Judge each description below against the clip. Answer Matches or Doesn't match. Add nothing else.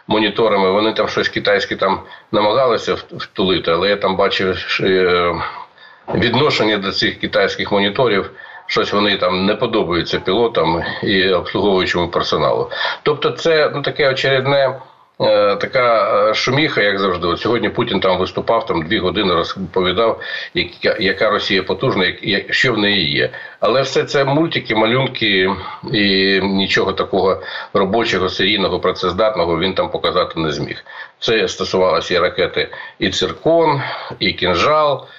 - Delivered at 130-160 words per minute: Matches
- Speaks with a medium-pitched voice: Doesn't match